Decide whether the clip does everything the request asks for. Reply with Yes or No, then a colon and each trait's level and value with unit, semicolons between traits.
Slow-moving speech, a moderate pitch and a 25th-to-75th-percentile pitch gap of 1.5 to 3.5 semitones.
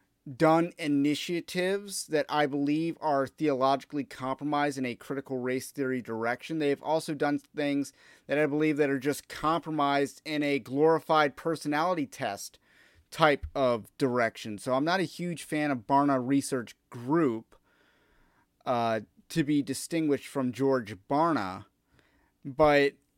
Yes: slow, 130 wpm; medium, 145 Hz; narrow, 2.5 semitones